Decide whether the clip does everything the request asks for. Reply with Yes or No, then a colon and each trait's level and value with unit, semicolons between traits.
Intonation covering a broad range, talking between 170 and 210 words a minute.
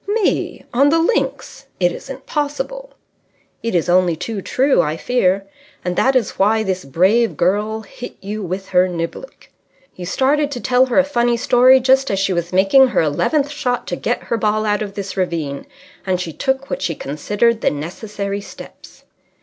Yes: wide, 6.1 semitones; average, 180 wpm